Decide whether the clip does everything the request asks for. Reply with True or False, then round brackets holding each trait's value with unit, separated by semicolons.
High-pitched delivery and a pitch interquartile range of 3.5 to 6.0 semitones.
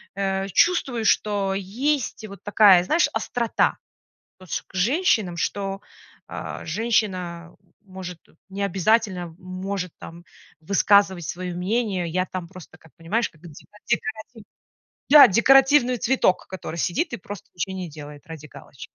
True (195 Hz; 3.8 semitones)